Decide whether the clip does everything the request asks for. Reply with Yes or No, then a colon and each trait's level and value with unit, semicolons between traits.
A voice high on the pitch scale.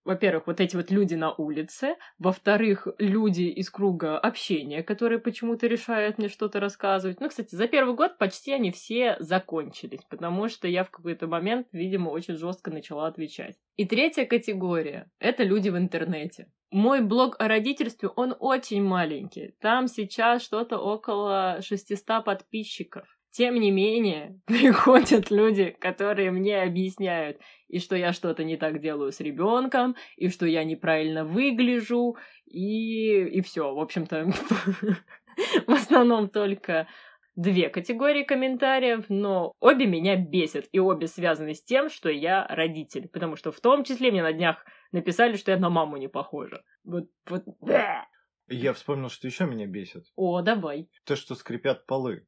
Yes: high, 195 Hz